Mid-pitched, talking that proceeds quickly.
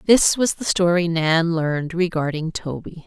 No: medium, 170 Hz; average, 155 wpm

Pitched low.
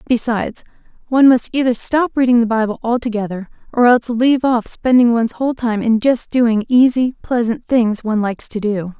No: high, 235 Hz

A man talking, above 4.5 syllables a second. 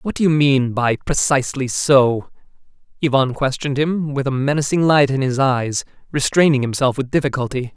Yes: male; 5.3 syllables/s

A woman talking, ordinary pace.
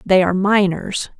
Yes: female; average, 150 wpm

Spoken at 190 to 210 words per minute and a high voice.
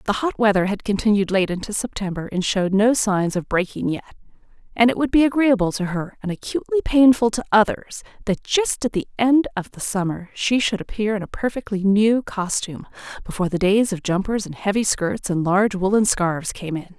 Yes: average, 200 wpm; high, 205 Hz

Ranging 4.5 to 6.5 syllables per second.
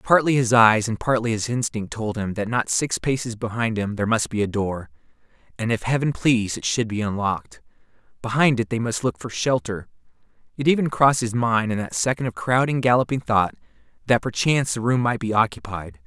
Yes: 5.6 syllables/s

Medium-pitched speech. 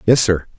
No: low, 105 Hz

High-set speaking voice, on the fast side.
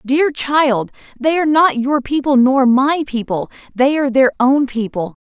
No: very high, 265 Hz; average, 170 wpm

